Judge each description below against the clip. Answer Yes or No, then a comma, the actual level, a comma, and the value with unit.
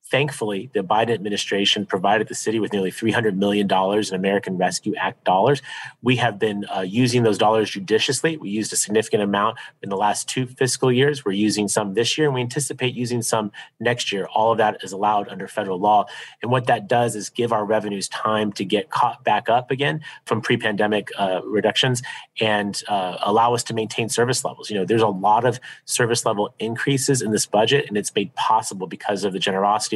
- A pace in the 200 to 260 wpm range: Yes, fast, 205 wpm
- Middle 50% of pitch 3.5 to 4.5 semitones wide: No, average, 2.8 semitones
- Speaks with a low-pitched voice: Yes, low, 110 Hz